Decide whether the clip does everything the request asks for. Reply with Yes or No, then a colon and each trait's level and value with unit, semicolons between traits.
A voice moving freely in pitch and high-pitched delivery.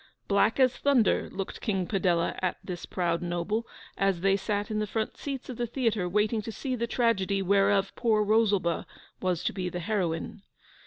No: average, 3.4 semitones; high, 200 Hz